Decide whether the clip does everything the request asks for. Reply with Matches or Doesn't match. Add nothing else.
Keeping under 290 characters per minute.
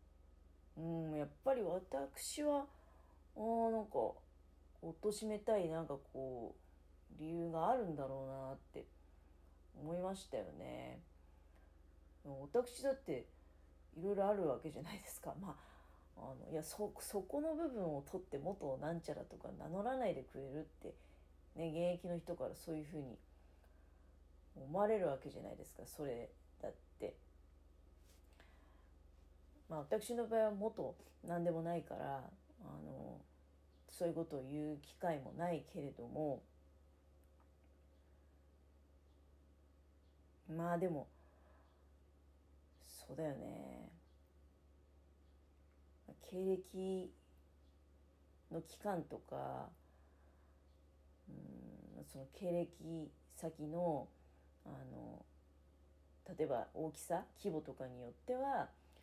Matches